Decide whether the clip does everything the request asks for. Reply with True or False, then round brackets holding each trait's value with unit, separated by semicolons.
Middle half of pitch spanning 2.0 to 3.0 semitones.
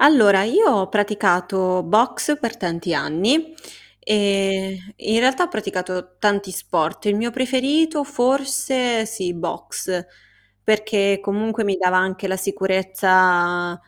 False (4.2 semitones)